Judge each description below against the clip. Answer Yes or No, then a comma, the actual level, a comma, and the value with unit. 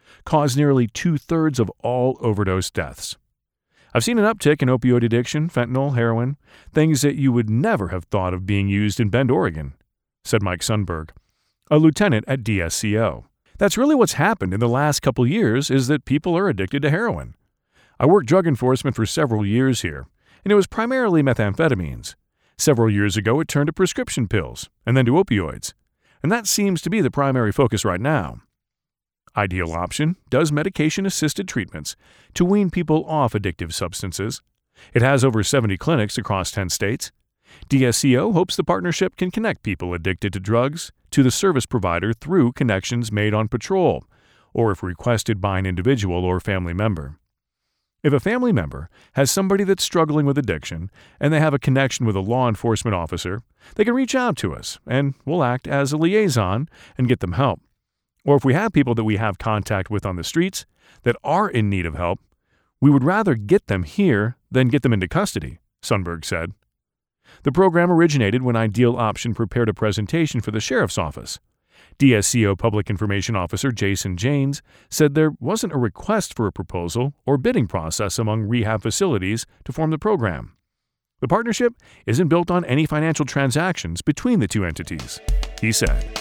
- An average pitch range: No, wide, 6.6 semitones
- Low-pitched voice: Yes, low, 120 Hz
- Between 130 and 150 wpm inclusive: No, average, 175 wpm